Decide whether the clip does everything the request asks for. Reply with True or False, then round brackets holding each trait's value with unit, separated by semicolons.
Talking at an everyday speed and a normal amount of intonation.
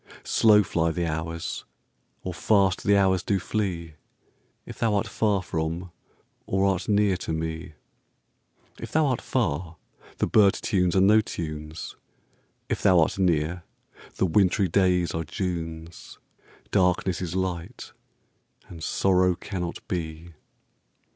False (120 wpm; 3.0 semitones)